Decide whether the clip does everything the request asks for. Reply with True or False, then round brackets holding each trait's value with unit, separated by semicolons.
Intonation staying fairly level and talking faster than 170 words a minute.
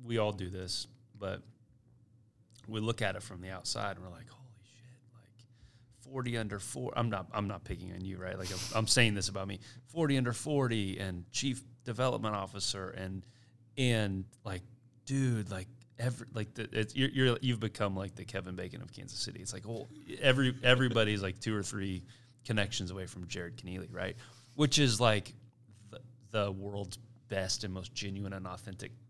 False (3.7 semitones; 190 wpm)